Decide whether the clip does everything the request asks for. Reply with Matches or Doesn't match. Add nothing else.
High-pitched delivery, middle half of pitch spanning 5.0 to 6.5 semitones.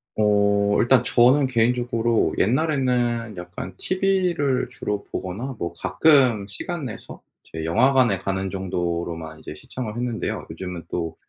Doesn't match